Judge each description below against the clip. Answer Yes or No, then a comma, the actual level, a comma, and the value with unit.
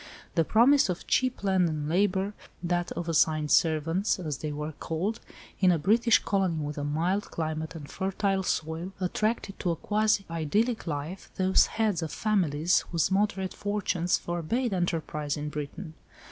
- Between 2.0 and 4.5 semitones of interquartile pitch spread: Yes, average, 4.1 semitones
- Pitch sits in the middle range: Yes, medium, 175 Hz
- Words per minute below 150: No, average, 160 wpm